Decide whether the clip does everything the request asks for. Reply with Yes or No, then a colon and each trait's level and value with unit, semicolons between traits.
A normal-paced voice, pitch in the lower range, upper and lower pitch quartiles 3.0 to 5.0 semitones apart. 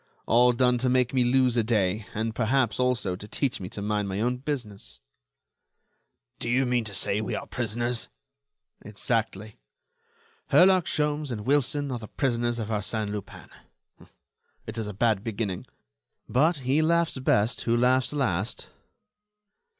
Yes: average, 150 wpm; low, 120 Hz; average, 3.5 semitones